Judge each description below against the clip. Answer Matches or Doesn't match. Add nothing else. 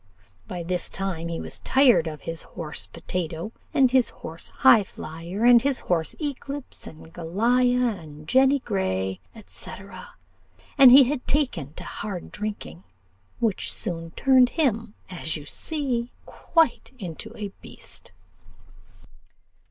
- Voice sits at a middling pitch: Doesn't match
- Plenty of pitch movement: Matches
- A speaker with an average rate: Doesn't match